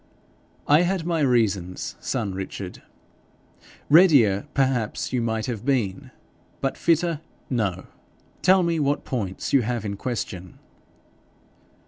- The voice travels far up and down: Yes, wide, 6.7 semitones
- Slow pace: Yes, slow, 115 wpm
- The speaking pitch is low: Yes, low, 120 Hz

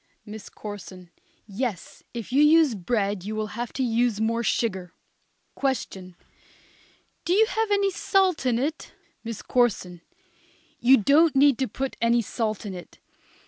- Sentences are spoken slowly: No, average, 145 wpm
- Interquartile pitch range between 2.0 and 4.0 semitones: No, average, 4.8 semitones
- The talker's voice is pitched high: Yes, high, 235 Hz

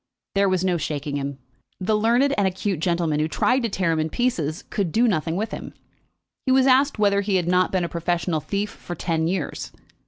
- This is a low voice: No, medium, 185 Hz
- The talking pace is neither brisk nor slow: No, fast, 215 wpm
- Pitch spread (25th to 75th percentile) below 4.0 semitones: No, average, 4.5 semitones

